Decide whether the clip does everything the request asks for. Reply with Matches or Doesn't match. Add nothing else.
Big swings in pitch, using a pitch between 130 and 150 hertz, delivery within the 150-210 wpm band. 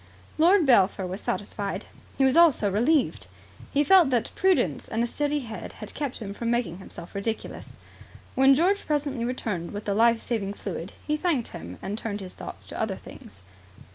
Doesn't match